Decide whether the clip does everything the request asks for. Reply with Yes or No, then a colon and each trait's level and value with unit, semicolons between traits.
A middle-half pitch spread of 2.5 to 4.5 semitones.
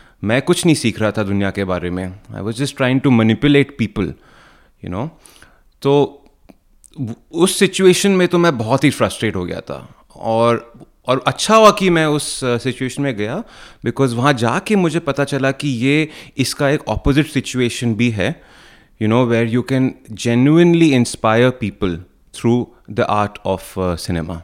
No: average, 5.0 semitones